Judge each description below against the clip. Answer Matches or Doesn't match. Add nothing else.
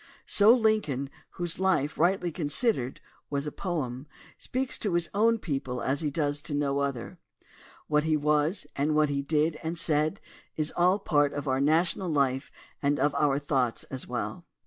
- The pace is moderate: Matches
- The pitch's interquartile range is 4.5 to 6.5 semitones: Doesn't match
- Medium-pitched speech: Matches